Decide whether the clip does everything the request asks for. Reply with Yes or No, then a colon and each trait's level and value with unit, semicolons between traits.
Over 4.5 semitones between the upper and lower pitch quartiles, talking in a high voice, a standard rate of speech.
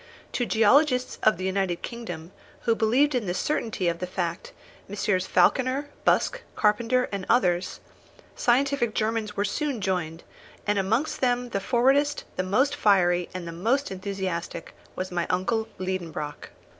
Yes: average, 5.2 semitones; high, 210 Hz; average, 150 wpm